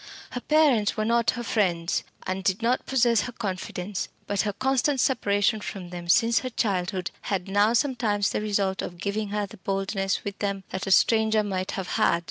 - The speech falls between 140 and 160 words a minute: No, average, 190 wpm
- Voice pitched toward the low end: No, high, 205 Hz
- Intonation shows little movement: No, average, 3.2 semitones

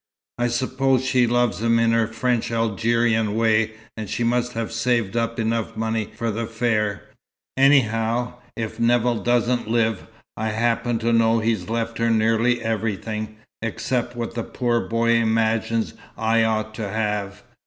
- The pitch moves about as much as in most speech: No, narrow, 1.2 semitones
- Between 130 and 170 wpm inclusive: Yes, average, 155 wpm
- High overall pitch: No, low, 115 Hz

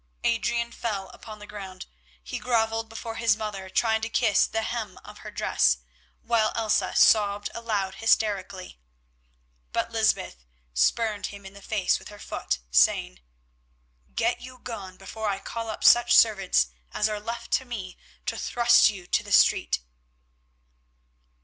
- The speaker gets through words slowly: No, average, 150 wpm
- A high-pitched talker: Yes, high, 215 Hz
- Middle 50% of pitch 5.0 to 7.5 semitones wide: No, average, 2.7 semitones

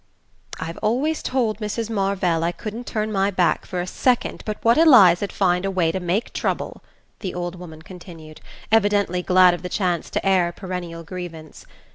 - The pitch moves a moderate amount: Yes, average, 3.3 semitones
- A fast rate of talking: No, average, 180 wpm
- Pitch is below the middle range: No, medium, 185 Hz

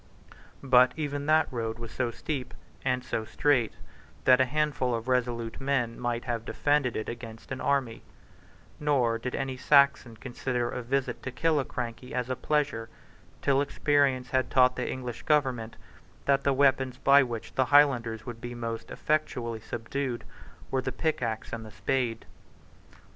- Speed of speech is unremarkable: Yes, average, 155 wpm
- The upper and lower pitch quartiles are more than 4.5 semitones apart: No, average, 2.9 semitones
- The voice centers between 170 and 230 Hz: No, low, 125 Hz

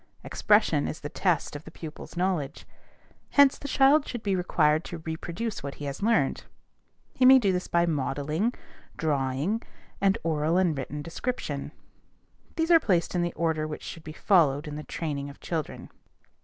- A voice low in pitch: No, medium, 165 Hz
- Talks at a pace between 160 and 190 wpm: Yes, average, 170 wpm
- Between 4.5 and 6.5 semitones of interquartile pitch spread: Yes, average, 5.1 semitones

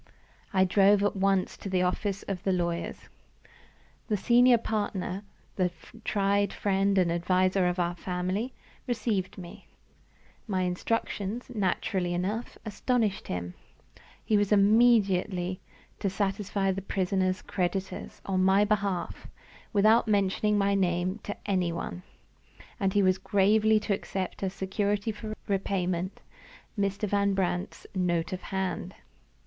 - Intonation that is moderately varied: No, narrow, 1.9 semitones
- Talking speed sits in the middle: No, slow, 130 wpm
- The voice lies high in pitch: Yes, high, 195 Hz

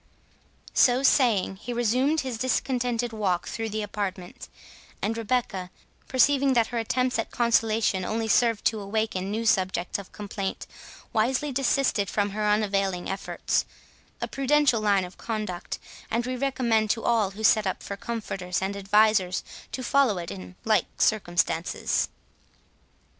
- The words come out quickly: No, average, 140 wpm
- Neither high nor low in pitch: No, high, 220 Hz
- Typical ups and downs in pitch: Yes, average, 3.6 semitones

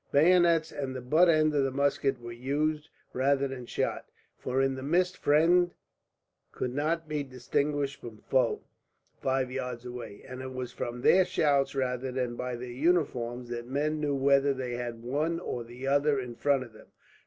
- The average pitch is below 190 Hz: Yes, low, 135 Hz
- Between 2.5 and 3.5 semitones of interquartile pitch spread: Yes, average, 3.2 semitones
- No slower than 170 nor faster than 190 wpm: Yes, average, 175 wpm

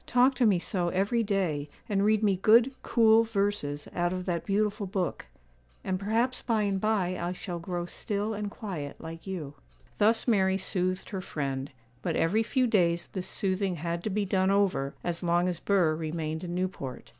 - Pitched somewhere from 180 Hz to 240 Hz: Yes, high, 190 Hz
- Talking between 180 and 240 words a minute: Yes, average, 185 wpm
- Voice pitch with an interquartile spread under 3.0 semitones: No, average, 3.4 semitones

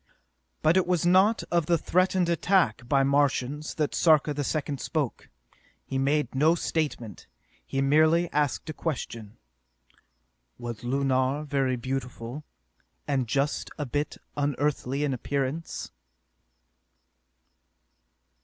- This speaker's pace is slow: Yes, slow, 115 wpm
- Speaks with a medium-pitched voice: Yes, medium, 145 Hz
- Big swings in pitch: No, average, 3.1 semitones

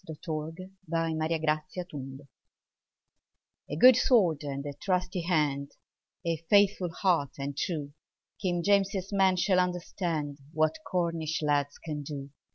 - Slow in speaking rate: Yes, slow, 110 wpm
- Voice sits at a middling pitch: Yes, medium, 165 Hz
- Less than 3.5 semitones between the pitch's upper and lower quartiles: No, average, 3.8 semitones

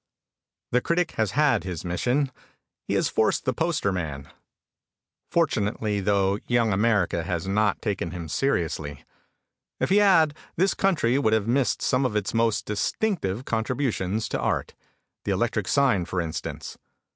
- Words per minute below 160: Yes, average, 145 wpm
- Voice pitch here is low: Yes, low, 110 Hz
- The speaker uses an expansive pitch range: Yes, wide, 6.1 semitones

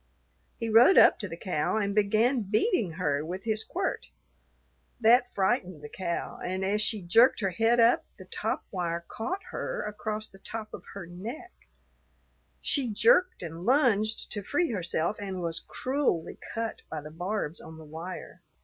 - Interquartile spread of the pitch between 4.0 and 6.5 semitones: Yes, average, 4.7 semitones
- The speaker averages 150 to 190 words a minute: Yes, average, 165 wpm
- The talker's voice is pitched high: Yes, high, 205 Hz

